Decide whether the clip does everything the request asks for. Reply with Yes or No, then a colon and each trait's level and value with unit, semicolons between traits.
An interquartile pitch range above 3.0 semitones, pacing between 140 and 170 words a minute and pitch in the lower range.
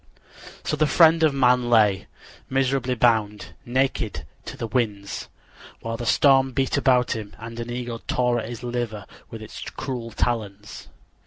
No: average, 2.7 semitones; average, 155 wpm; low, 120 Hz